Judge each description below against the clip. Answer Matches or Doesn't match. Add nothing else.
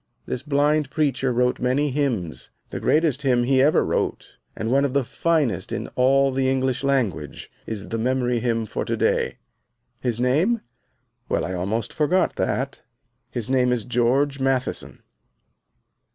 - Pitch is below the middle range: Matches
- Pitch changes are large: Doesn't match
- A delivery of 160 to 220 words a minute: Doesn't match